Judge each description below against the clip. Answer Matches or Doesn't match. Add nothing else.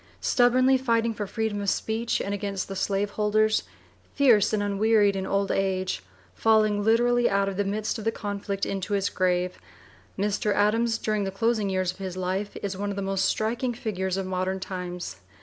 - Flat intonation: Matches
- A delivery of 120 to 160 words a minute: Doesn't match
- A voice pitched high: Matches